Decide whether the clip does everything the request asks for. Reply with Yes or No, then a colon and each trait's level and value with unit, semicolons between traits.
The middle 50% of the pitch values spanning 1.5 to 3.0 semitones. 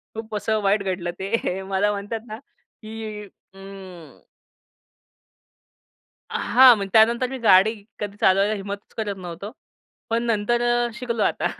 Yes: narrow, 2.4 semitones